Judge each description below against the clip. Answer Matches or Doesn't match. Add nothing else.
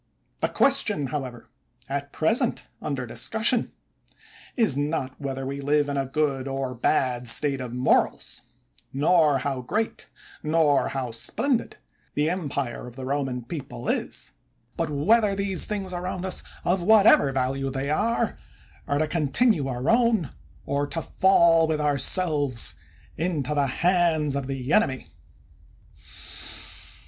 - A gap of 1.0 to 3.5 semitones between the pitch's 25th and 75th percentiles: Doesn't match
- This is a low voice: Doesn't match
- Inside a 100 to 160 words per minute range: Matches